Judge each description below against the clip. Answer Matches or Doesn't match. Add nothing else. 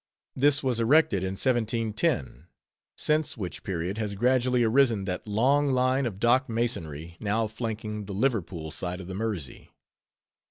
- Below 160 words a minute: Matches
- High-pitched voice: Doesn't match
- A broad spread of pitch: Doesn't match